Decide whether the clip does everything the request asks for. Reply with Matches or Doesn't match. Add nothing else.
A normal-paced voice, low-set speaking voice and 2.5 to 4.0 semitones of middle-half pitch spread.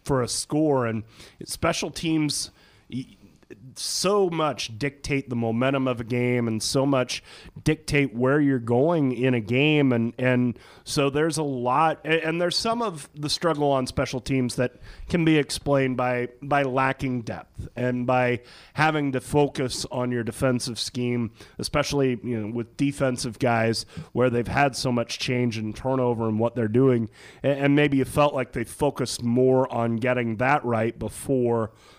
Matches